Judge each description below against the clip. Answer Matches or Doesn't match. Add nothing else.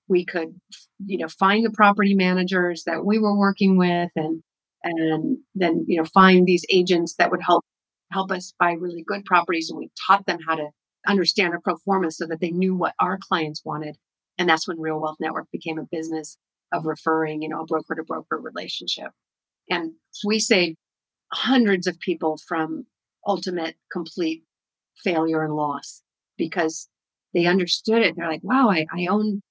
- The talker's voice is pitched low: Doesn't match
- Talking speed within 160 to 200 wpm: Matches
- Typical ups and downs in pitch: Matches